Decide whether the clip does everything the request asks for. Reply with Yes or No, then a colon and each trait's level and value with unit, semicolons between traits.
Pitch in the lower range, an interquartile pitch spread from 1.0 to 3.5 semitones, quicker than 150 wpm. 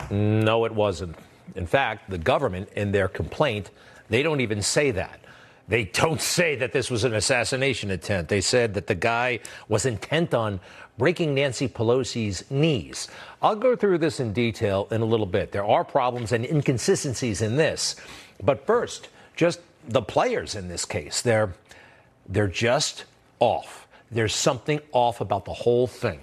No: low, 115 Hz; average, 4.2 semitones; average, 165 wpm